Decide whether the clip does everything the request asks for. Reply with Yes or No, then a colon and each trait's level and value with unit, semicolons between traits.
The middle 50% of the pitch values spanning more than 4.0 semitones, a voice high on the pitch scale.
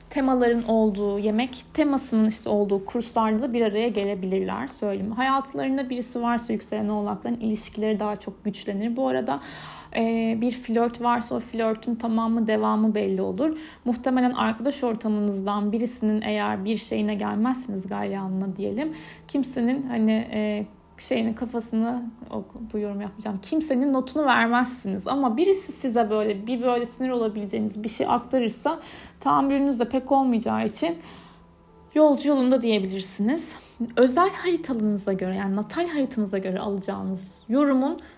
No: average, 3.6 semitones; high, 230 Hz